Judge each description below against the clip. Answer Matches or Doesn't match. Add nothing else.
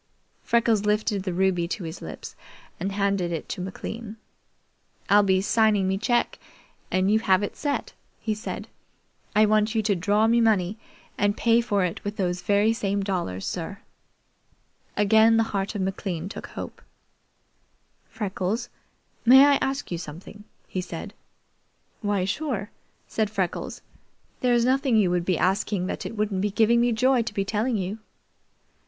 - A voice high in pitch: Matches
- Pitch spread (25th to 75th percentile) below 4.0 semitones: Matches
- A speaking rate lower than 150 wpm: Doesn't match